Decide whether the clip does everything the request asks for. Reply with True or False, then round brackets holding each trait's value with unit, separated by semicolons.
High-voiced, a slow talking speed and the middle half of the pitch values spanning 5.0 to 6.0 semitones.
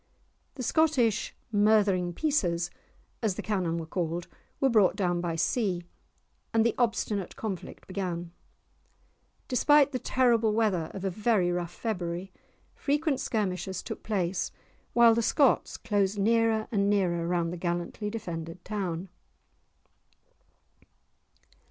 False (200 Hz; 120 wpm; 4.4 semitones)